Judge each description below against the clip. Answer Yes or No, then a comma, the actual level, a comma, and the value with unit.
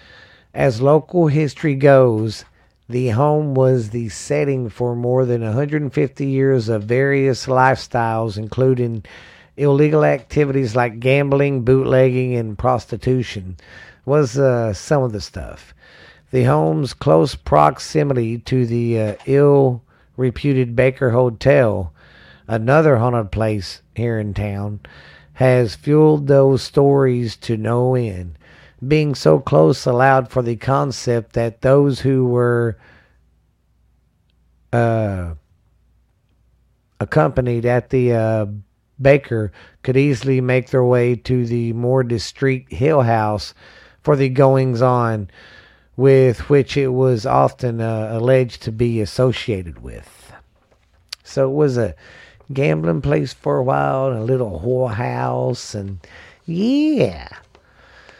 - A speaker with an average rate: No, slow, 120 wpm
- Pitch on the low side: Yes, low, 125 Hz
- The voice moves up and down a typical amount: Yes, average, 3.5 semitones